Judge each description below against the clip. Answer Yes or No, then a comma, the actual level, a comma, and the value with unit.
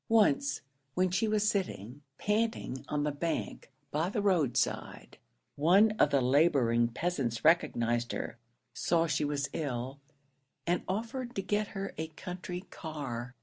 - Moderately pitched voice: Yes, medium, 160 Hz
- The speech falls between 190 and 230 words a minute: No, average, 145 wpm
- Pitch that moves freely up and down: Yes, wide, 6.6 semitones